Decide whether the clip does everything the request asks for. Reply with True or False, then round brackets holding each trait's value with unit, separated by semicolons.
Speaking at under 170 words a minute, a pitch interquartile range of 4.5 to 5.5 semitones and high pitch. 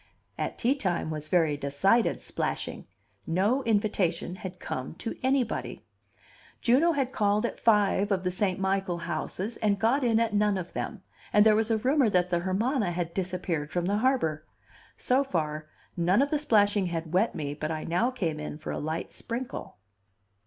False (180 wpm; 5.1 semitones; 195 Hz)